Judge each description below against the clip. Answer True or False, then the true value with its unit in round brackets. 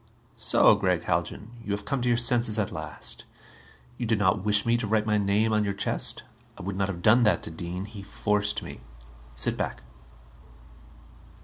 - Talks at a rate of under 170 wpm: False (190 wpm)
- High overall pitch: False (105 Hz)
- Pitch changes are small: True (1.9 semitones)